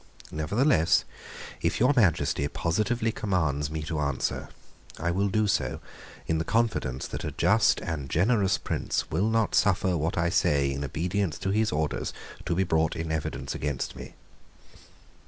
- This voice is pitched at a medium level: No, very low, 85 Hz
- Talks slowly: No, average, 155 wpm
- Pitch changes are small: No, average, 4.9 semitones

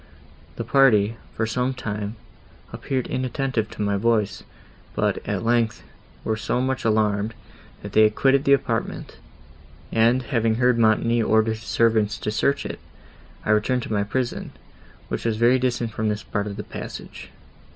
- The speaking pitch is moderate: No, low, 115 Hz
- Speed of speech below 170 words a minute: Yes, average, 160 wpm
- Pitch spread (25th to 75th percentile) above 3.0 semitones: No, narrow, 2.6 semitones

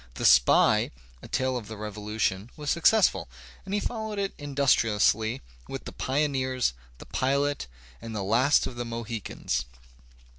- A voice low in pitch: Yes, low, 125 Hz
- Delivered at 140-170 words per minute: Yes, average, 145 wpm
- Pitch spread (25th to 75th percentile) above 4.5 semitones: Yes, average, 5.1 semitones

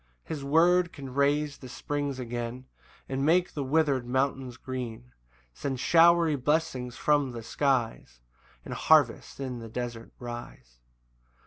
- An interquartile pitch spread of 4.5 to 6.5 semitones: No, average, 3.4 semitones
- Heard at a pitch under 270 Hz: Yes, low, 135 Hz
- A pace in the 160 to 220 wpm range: No, slow, 135 wpm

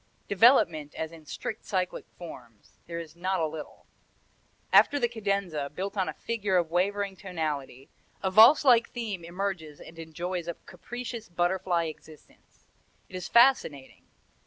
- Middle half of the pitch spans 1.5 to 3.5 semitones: No, average, 4.0 semitones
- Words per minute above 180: No, average, 145 wpm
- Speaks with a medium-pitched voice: Yes, medium, 180 Hz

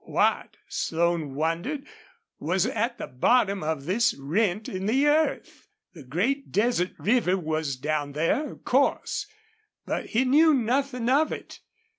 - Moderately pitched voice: No, high, 200 Hz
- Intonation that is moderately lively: No, wide, 8.2 semitones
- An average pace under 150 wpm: Yes, average, 140 wpm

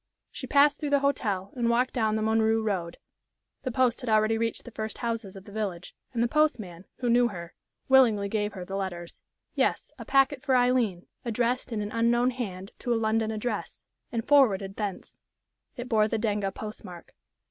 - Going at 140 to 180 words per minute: No, average, 190 wpm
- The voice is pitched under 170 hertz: No, high, 220 Hz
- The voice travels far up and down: No, average, 3.4 semitones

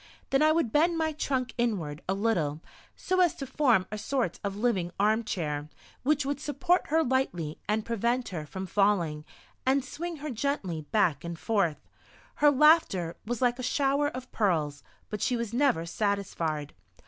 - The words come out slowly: No, average, 170 wpm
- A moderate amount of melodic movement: No, wide, 8.0 semitones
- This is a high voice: Yes, high, 230 Hz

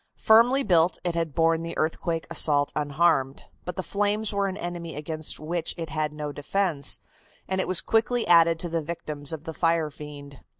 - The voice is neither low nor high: Yes, medium, 165 Hz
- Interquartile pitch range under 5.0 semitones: Yes, average, 2.8 semitones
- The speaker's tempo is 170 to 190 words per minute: Yes, average, 185 wpm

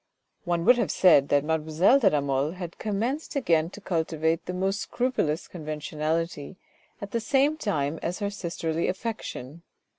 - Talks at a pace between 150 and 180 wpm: Yes, average, 155 wpm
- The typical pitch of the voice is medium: Yes, medium, 170 Hz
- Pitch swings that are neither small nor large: Yes, average, 4.7 semitones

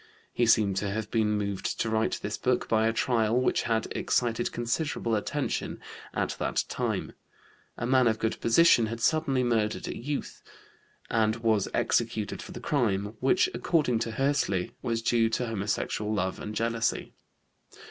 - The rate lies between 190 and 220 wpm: No, average, 160 wpm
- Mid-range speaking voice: No, low, 115 Hz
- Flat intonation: Yes, narrow, 2.1 semitones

